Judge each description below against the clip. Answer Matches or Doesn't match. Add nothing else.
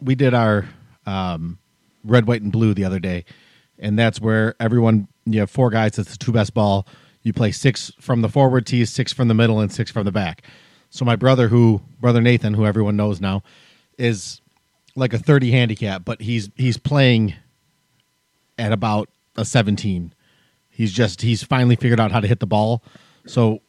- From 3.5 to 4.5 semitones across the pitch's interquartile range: Doesn't match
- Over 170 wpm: Matches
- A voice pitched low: Matches